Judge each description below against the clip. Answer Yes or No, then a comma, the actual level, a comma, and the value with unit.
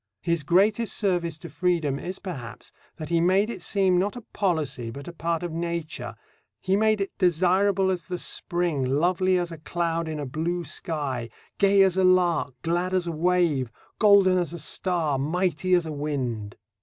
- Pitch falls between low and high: Yes, medium, 175 Hz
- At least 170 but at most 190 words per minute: Yes, average, 180 wpm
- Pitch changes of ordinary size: Yes, average, 3.1 semitones